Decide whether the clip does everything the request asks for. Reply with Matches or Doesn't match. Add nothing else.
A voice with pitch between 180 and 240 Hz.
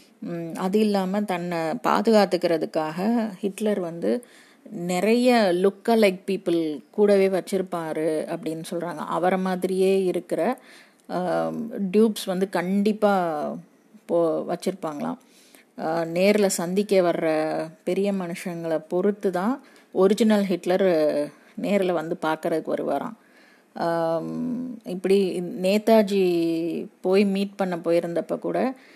Matches